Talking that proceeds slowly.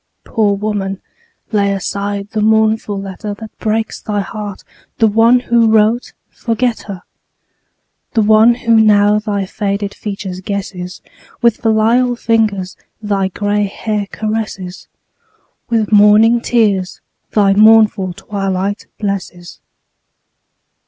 Yes: slow, 110 wpm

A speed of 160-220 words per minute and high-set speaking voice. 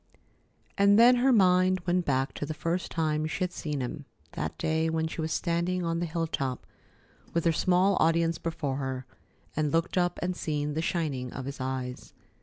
No: average, 195 wpm; medium, 165 Hz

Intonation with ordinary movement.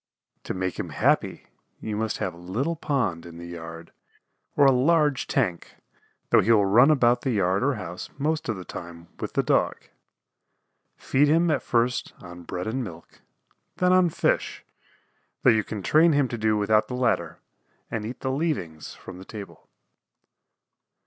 No: wide, 7.2 semitones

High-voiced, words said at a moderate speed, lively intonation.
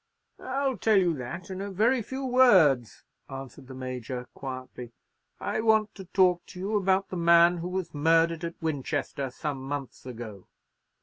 No: medium, 170 Hz; average, 165 wpm; wide, 6.6 semitones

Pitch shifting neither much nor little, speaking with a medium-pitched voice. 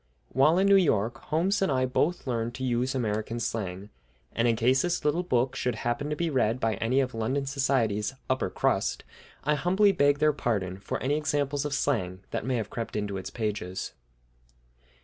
No: average, 4.7 semitones; low, 130 Hz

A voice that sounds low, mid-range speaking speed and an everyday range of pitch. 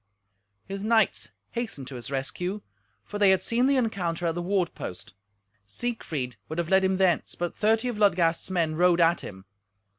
No: medium, 180 Hz; average, 180 wpm; average, 4.2 semitones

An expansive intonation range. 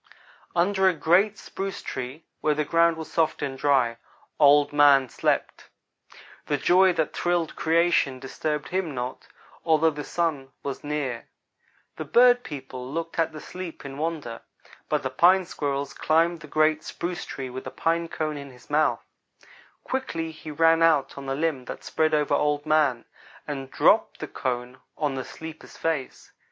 No: average, 3.2 semitones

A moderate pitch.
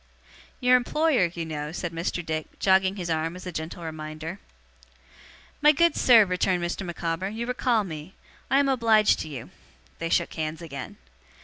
Yes: medium, 175 Hz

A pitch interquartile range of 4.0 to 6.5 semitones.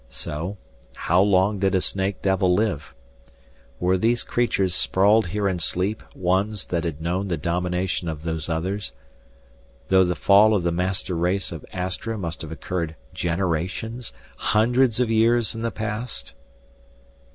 No: average, 3.5 semitones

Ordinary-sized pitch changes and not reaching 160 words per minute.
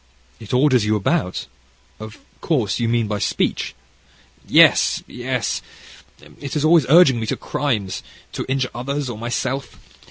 Yes: average, 4.0 semitones; average, 145 wpm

